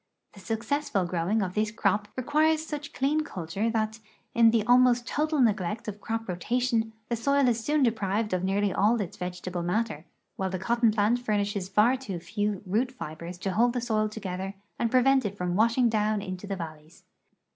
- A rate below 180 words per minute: No, average, 185 wpm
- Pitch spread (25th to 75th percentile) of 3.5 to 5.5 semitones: Yes, average, 4.0 semitones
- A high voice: Yes, high, 215 Hz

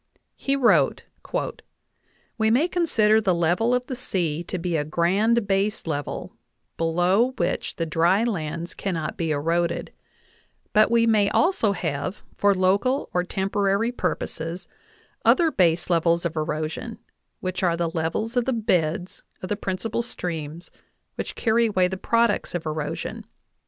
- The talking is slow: No, average, 145 wpm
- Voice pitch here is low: No, medium, 185 Hz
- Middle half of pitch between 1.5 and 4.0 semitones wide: No, average, 5.0 semitones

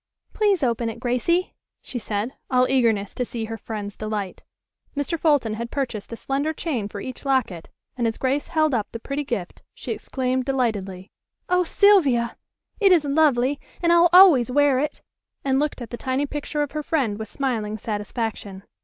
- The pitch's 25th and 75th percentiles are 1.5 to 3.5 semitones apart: No, average, 4.6 semitones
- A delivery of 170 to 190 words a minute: Yes, average, 180 wpm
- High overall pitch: Yes, very high, 255 Hz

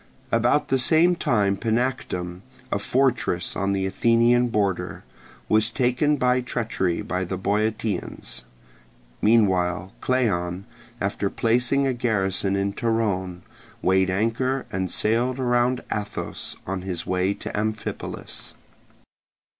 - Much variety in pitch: No, average, 4.4 semitones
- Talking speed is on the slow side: Yes, slow, 115 wpm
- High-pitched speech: No, low, 110 Hz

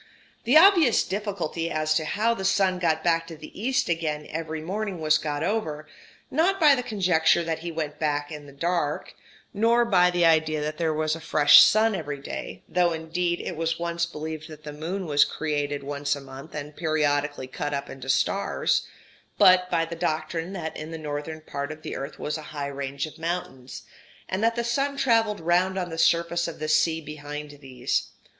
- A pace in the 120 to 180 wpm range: No, average, 200 wpm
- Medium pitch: Yes, medium, 160 Hz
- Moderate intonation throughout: Yes, average, 3.2 semitones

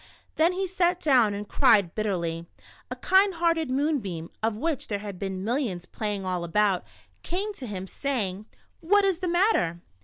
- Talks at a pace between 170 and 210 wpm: Yes, average, 180 wpm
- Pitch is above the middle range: Yes, high, 225 Hz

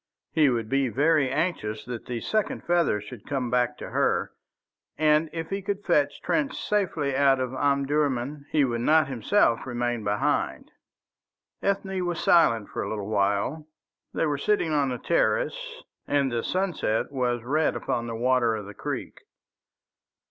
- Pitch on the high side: No, medium, 140 Hz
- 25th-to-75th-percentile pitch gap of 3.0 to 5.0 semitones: No, wide, 5.4 semitones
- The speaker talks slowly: No, average, 160 wpm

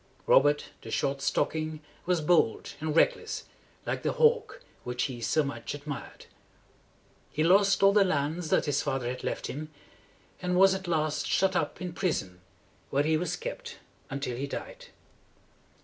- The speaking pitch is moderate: Yes, medium, 155 Hz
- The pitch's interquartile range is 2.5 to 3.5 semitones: No, average, 4.6 semitones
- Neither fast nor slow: Yes, average, 160 wpm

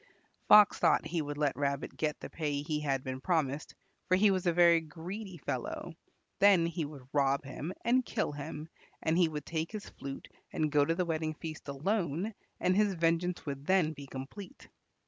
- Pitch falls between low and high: Yes, medium, 160 Hz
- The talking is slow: No, average, 190 wpm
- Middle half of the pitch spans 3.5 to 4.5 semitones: Yes, average, 4.0 semitones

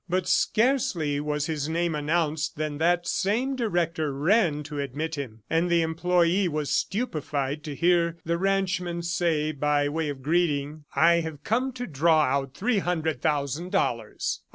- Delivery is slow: No, average, 155 wpm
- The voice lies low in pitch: No, medium, 160 Hz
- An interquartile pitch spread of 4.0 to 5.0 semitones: No, average, 3.1 semitones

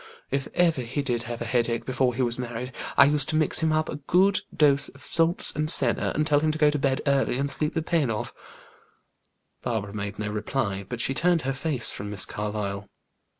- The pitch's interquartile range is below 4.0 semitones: No, average, 4.6 semitones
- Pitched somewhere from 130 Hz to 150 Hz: Yes, low, 135 Hz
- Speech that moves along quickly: Yes, fast, 220 wpm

